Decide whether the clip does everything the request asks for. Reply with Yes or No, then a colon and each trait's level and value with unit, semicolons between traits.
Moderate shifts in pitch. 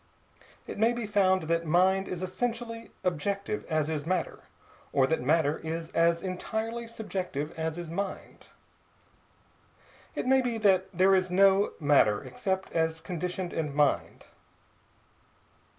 Yes: average, 3.7 semitones